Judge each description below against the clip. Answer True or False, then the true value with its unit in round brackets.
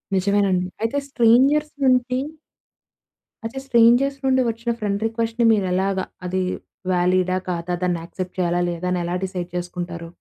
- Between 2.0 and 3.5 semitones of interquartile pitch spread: False (4.6 semitones)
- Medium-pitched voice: False (195 Hz)